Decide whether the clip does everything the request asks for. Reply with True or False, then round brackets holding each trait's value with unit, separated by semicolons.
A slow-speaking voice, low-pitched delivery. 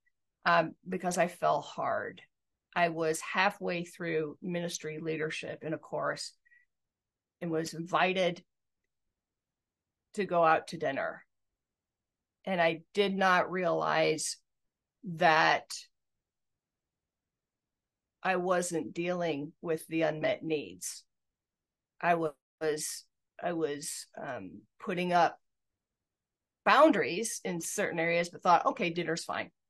False (105 wpm; 170 Hz)